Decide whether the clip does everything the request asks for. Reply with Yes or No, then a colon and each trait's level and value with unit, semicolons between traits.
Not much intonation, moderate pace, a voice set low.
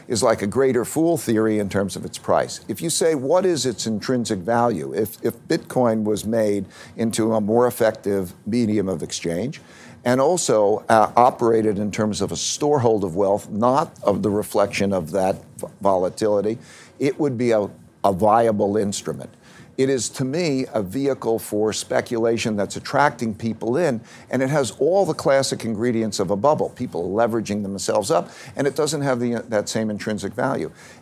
No: average, 3.7 semitones; average, 180 wpm; low, 115 Hz